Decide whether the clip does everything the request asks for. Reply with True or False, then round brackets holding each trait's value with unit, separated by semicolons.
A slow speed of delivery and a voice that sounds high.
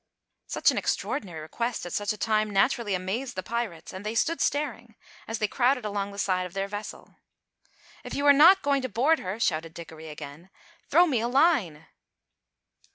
False (185 wpm; 215 Hz)